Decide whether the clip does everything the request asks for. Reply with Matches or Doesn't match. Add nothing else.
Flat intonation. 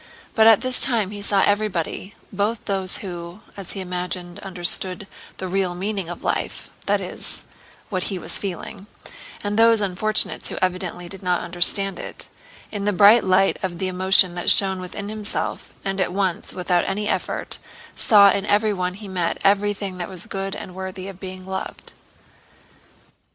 Matches